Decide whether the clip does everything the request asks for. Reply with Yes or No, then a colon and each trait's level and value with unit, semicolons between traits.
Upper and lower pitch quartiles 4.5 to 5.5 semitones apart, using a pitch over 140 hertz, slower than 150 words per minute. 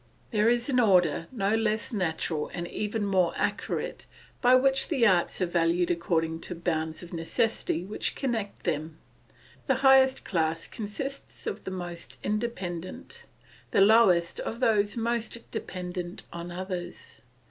Yes: average, 5.2 semitones; high, 190 Hz; average, 140 wpm